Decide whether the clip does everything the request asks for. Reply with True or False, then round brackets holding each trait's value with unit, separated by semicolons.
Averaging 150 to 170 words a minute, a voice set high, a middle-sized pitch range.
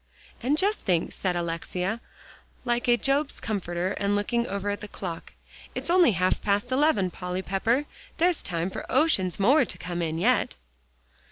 False (165 wpm; 205 Hz; 5.7 semitones)